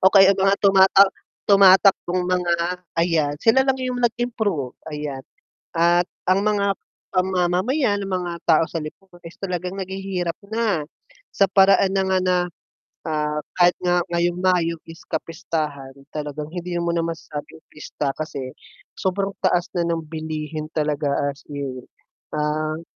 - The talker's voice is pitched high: No, medium, 175 Hz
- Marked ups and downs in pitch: No, average, 3.7 semitones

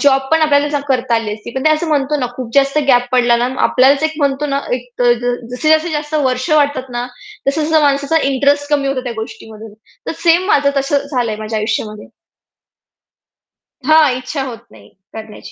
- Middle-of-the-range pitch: No, very high, 270 Hz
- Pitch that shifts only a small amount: No, average, 3.4 semitones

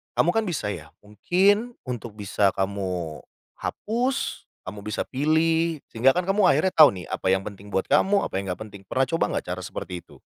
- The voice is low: Yes, low, 120 Hz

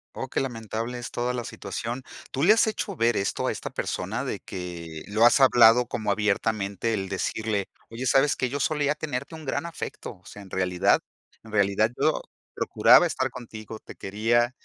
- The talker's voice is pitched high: No, low, 115 Hz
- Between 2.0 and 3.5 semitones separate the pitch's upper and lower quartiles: No, average, 4.0 semitones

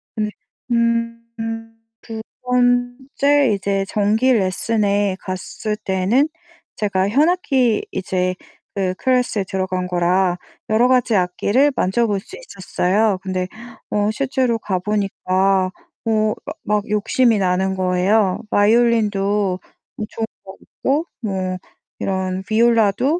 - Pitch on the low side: No, high, 210 Hz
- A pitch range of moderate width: Yes, average, 3.8 semitones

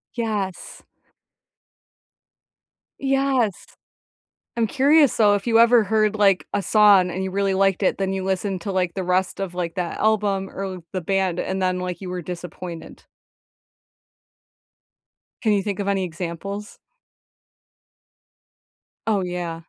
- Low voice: No, high, 195 Hz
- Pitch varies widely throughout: No, narrow, 2.4 semitones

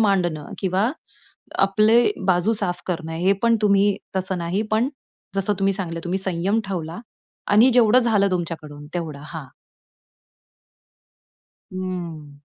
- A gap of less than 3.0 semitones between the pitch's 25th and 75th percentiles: No, average, 3.7 semitones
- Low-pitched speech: No, medium, 185 Hz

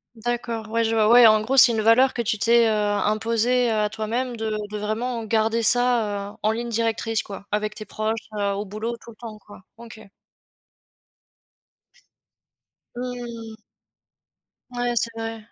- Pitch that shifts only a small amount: Yes, narrow, 1.6 semitones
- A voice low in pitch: No, high, 225 Hz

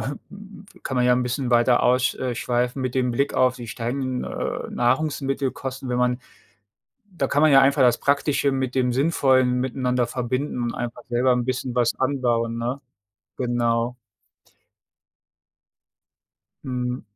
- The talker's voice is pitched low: Yes, low, 125 Hz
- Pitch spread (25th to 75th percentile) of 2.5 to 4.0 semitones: No, narrow, 1.7 semitones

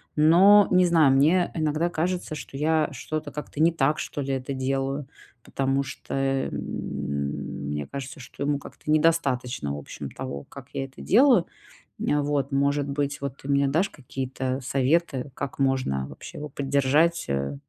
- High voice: No, medium, 140 Hz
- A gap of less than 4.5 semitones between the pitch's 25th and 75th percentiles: Yes, average, 2.7 semitones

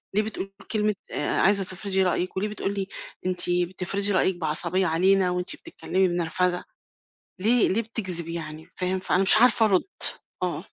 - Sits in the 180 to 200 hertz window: Yes, medium, 185 Hz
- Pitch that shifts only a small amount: Yes, narrow, 2.1 semitones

